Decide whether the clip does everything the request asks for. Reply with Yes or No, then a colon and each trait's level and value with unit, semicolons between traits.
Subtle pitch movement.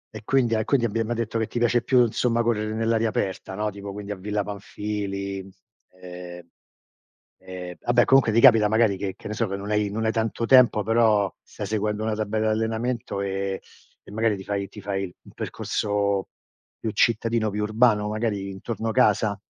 Yes: narrow, 2.2 semitones